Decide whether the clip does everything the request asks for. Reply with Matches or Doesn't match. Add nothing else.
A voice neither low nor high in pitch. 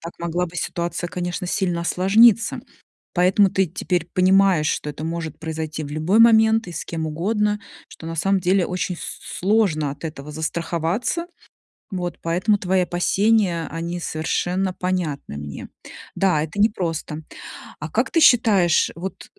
Matches